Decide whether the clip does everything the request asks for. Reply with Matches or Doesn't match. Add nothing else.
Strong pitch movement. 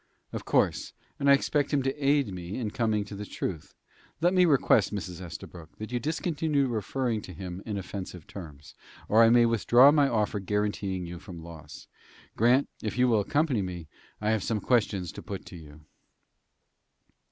Matches